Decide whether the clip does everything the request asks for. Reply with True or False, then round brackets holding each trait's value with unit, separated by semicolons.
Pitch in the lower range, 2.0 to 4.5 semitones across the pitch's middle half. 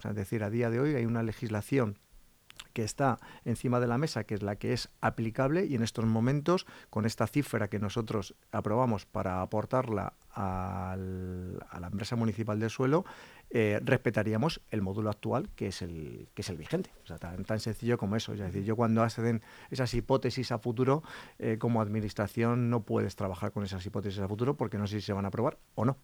True (110 Hz; 2.8 semitones)